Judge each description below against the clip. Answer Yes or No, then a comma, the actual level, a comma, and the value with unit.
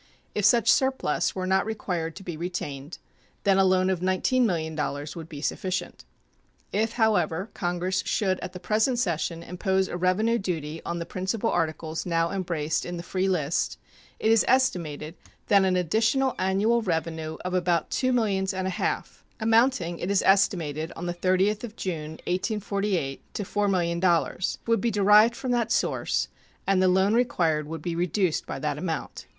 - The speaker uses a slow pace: No, average, 165 wpm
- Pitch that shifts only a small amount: No, average, 3.8 semitones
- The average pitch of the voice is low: No, medium, 185 Hz